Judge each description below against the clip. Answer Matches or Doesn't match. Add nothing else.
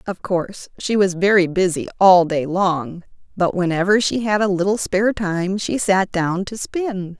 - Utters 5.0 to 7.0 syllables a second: Doesn't match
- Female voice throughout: Matches